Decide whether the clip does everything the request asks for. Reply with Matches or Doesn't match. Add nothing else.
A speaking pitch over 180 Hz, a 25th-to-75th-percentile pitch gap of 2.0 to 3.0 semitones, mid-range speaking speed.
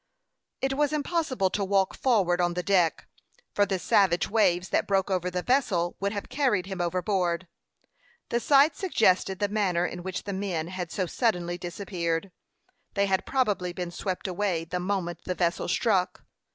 Matches